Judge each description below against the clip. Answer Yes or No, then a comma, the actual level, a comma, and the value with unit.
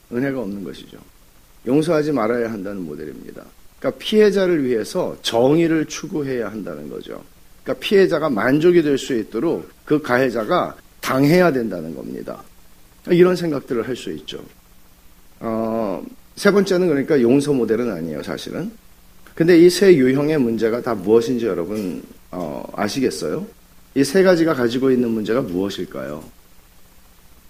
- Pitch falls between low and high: No, low, 130 Hz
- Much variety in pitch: Yes, wide, 8.8 semitones